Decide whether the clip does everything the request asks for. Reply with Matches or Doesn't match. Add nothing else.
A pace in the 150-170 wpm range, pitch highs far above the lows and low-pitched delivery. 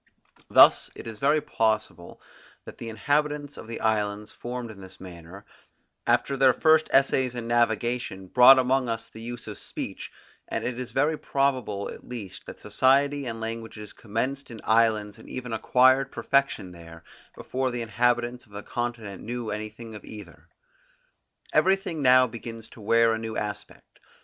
Doesn't match